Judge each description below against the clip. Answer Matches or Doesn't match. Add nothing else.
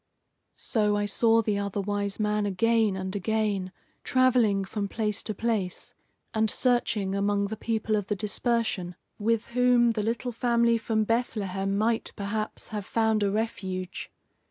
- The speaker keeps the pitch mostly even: Matches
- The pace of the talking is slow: Doesn't match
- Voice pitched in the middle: Doesn't match